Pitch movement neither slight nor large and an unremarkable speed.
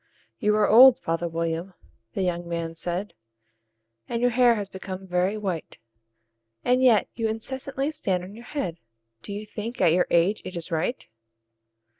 Yes: average, 5.0 semitones; average, 165 wpm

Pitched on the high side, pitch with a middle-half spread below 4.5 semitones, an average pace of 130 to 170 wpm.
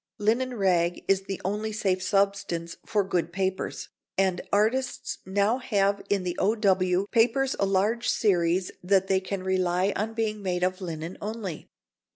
Yes: high, 195 Hz; narrow, 2.5 semitones; average, 155 wpm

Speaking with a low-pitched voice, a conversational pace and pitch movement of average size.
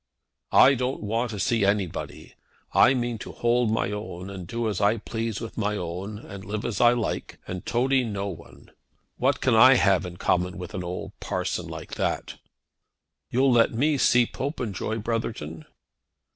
Yes: low, 110 Hz; average, 170 wpm; average, 3.6 semitones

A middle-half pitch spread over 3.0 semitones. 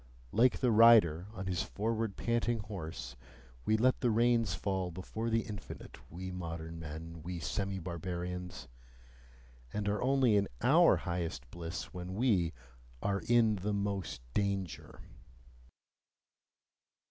Yes: average, 4.2 semitones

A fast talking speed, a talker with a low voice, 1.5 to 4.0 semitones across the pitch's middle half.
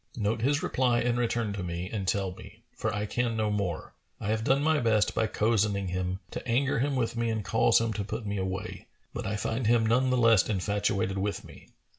Yes: fast, 225 wpm; low, 110 Hz; average, 3.0 semitones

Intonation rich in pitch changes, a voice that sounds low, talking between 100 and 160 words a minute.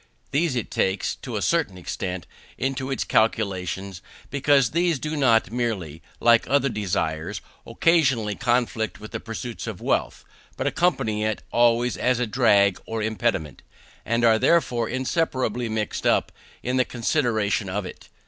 No: average, 3.8 semitones; low, 115 Hz; average, 150 wpm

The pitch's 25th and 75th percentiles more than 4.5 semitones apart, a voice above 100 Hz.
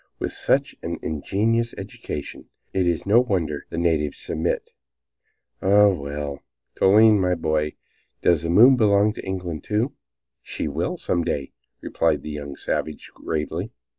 No: average, 5.2 semitones; very low, 85 Hz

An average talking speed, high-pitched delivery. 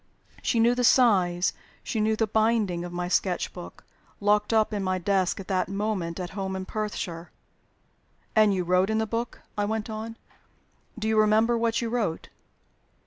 Yes: average, 180 wpm; high, 210 Hz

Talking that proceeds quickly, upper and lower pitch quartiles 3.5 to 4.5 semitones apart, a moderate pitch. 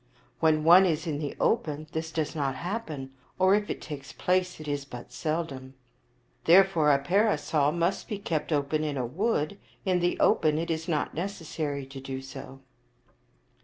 No: average, 170 wpm; average, 3.8 semitones; medium, 155 Hz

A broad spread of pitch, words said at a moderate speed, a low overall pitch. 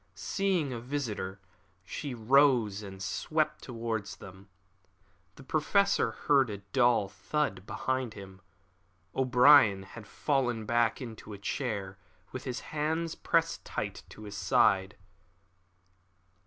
No: wide, 5.9 semitones; slow, 115 wpm; low, 120 Hz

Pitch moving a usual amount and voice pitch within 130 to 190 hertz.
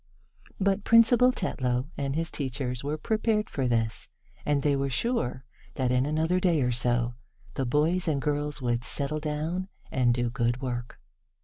Yes: average, 4.9 semitones; medium, 140 Hz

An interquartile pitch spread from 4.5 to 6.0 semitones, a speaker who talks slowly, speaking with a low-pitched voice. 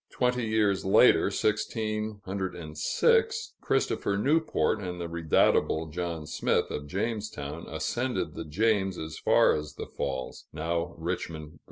Yes: average, 5.3 semitones; slow, 125 wpm; very low, 90 Hz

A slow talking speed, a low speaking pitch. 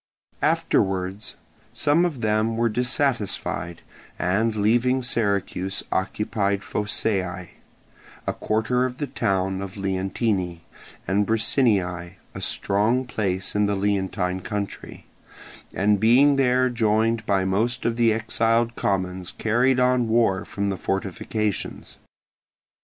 Yes: slow, 115 wpm; low, 105 Hz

